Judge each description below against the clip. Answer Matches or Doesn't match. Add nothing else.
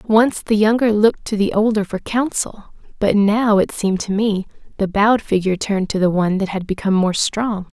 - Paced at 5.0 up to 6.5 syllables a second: Matches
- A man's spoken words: Doesn't match